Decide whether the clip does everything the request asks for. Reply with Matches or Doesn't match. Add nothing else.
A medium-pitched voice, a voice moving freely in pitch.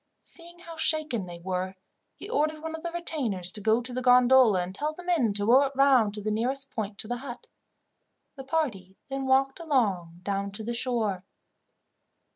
Doesn't match